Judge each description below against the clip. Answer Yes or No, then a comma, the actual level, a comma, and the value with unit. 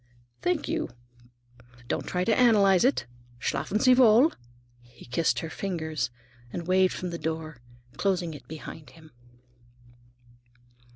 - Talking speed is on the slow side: Yes, slow, 125 wpm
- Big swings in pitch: No, average, 4.2 semitones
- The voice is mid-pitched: Yes, medium, 170 Hz